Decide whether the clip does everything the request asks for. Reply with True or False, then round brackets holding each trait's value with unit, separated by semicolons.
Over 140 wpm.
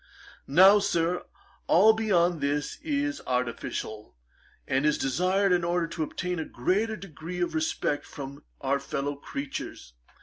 False (135 wpm)